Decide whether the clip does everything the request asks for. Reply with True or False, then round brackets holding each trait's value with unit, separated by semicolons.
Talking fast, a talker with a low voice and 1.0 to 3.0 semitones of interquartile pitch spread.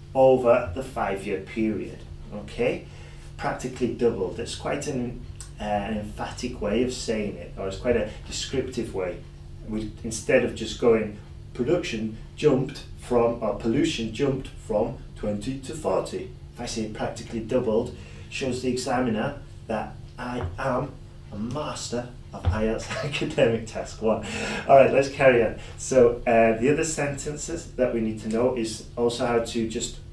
False (150 wpm; 115 Hz; 2.4 semitones)